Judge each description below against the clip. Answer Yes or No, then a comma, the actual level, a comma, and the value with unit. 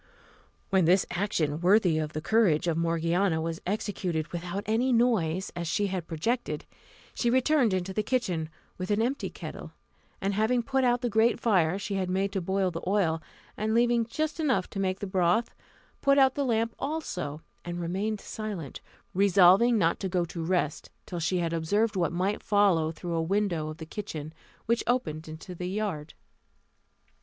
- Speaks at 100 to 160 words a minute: No, average, 180 wpm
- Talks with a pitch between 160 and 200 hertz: Yes, high, 190 Hz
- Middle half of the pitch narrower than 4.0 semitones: No, average, 4.7 semitones